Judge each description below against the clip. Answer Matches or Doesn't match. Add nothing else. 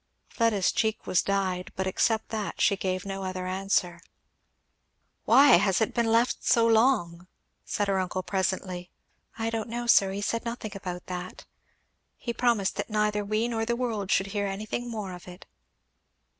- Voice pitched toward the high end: Matches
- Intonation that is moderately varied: Matches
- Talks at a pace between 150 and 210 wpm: Matches